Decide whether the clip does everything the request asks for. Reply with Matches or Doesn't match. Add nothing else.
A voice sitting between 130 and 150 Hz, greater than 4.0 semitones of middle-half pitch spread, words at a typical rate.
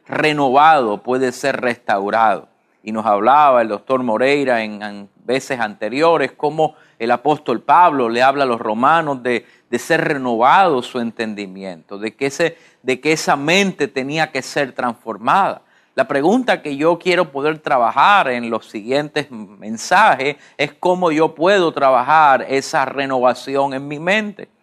Matches